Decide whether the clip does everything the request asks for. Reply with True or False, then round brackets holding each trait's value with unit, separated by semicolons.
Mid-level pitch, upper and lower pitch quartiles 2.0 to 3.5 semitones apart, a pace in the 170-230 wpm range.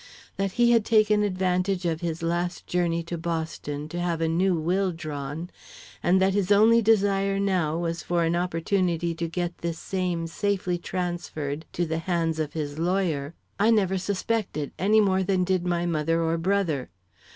True (175 Hz; 2.7 semitones; 175 wpm)